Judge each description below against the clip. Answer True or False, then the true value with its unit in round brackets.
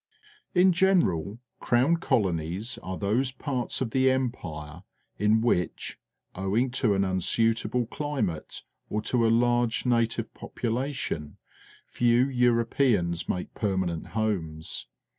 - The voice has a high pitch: False (115 Hz)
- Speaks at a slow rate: True (110 wpm)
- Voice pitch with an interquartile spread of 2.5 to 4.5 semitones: False (5.1 semitones)